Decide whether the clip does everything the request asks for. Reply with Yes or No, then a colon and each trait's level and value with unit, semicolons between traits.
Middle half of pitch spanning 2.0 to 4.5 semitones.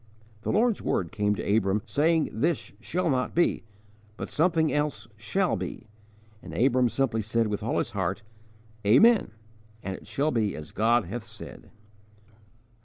No: wide, 5.6 semitones